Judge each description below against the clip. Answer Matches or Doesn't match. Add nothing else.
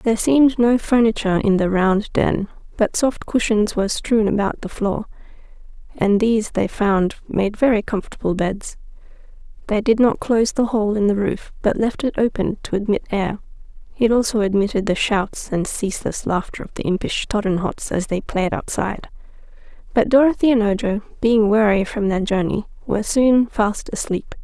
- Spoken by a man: Doesn't match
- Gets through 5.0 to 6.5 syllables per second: Matches